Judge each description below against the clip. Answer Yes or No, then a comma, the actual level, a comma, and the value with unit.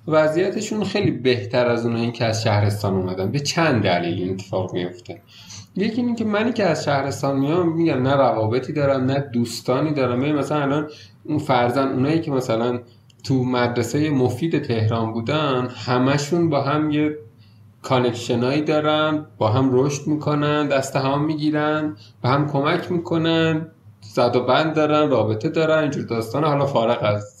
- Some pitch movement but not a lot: Yes, average, 4.5 semitones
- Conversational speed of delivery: No, fast, 160 wpm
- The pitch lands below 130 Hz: No, low, 135 Hz